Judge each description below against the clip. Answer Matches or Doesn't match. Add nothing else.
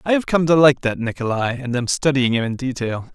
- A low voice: Matches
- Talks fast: Matches